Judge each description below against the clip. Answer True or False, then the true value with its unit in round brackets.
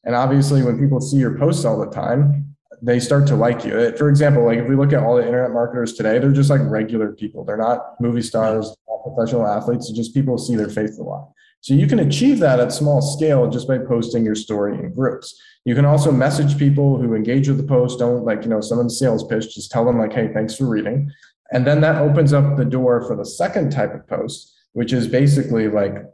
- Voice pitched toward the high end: False (125 Hz)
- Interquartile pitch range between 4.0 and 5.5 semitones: False (3.4 semitones)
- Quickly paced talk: True (240 wpm)